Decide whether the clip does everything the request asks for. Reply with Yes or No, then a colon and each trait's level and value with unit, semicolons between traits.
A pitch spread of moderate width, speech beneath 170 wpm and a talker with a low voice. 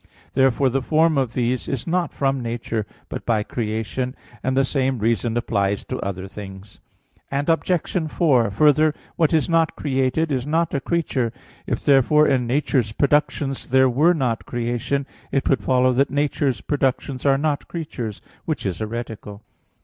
Yes: average, 3.9 semitones; average, 155 wpm; low, 130 Hz